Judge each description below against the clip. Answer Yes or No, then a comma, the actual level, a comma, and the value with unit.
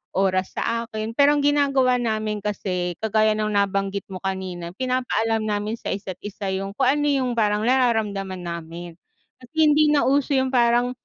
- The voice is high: Yes, high, 215 Hz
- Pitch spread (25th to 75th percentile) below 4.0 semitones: No, average, 4.6 semitones